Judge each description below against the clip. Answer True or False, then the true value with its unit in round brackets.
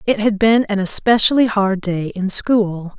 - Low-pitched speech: False (205 Hz)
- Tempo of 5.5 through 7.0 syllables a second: False (4.2 syllables/s)